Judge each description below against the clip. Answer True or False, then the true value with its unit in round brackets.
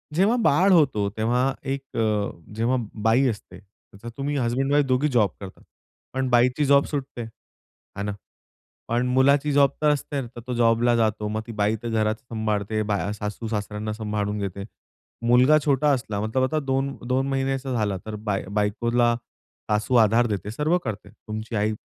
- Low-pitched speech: True (120 Hz)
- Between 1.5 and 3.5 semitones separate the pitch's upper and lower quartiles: False (3.9 semitones)